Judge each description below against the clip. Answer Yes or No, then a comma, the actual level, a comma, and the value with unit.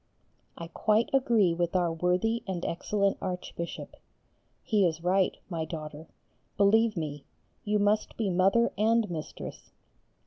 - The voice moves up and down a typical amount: Yes, average, 4.0 semitones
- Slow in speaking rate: Yes, slow, 130 wpm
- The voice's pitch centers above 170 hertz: Yes, medium, 185 Hz